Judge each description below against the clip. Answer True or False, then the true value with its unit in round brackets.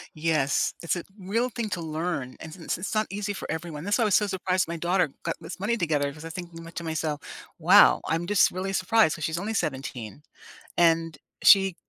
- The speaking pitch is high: False (170 Hz)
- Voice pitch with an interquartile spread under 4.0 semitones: True (3.3 semitones)